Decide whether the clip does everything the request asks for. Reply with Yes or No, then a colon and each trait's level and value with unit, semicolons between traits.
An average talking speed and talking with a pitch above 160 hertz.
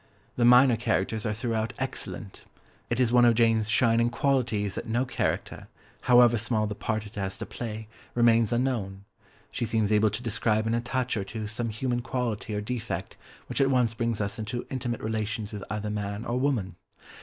No: average, 190 wpm; low, 115 Hz